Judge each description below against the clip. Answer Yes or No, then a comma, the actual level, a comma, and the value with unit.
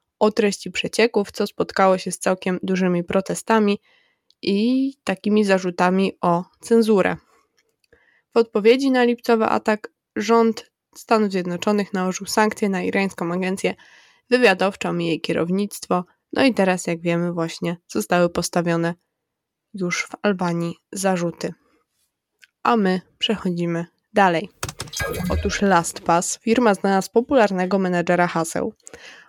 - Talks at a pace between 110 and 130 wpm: Yes, average, 115 wpm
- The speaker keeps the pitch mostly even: No, average, 4.0 semitones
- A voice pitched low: No, high, 190 Hz